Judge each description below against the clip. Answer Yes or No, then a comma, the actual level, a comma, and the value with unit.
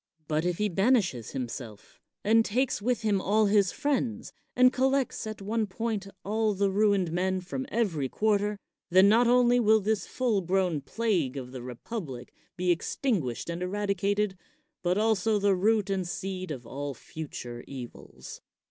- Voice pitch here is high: Yes, high, 200 Hz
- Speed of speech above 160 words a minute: No, average, 155 wpm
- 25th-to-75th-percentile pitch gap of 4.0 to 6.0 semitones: Yes, average, 4.3 semitones